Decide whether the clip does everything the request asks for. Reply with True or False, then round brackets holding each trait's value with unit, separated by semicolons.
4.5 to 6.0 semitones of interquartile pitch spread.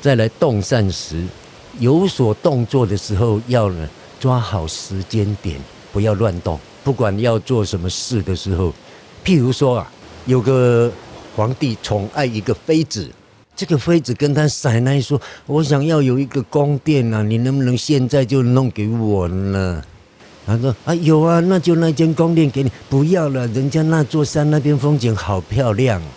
True (5.5 semitones)